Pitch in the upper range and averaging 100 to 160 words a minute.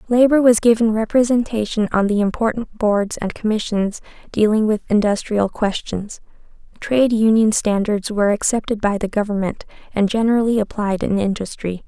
Yes: high, 215 Hz; slow, 135 wpm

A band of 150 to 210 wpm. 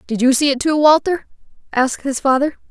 Yes: average, 200 wpm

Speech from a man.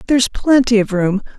No: female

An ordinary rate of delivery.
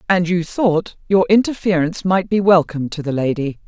Yes: average, 180 wpm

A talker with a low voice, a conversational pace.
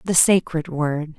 No: medium, 165 Hz; average, 150 wpm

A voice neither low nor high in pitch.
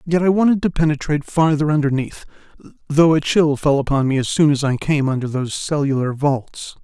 Yes: medium, 145 Hz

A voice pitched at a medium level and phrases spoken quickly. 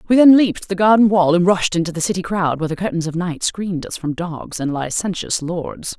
Yes: medium, 175 Hz; fast, 240 wpm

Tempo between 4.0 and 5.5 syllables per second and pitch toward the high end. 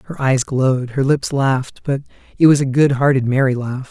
No: 5.4 syllables/s; low, 135 Hz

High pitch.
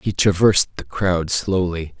No: very low, 90 Hz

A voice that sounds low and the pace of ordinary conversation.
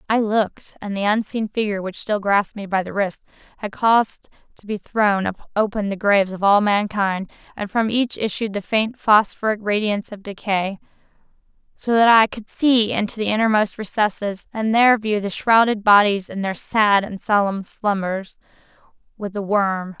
No: high, 205 Hz; average, 175 wpm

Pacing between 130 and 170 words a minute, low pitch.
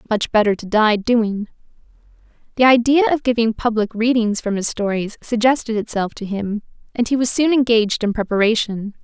No: average, 165 wpm; high, 225 Hz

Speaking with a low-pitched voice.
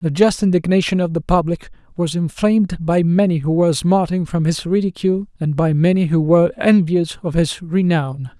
No: medium, 170 Hz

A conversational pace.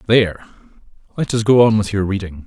Yes: average, 195 wpm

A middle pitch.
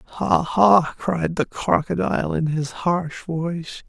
Yes: medium, 170 Hz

